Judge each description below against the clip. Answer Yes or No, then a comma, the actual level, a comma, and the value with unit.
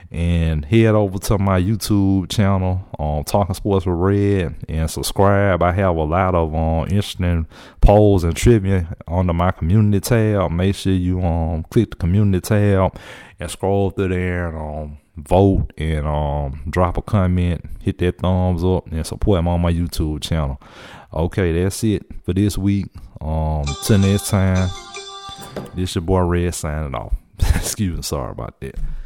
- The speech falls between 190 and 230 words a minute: No, average, 170 wpm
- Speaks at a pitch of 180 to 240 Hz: No, very low, 90 Hz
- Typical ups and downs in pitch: Yes, average, 3.5 semitones